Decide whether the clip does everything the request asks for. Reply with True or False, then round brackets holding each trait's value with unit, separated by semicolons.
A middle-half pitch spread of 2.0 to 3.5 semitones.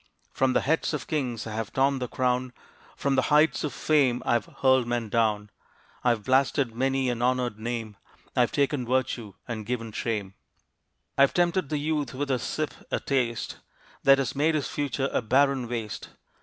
True (3.0 semitones)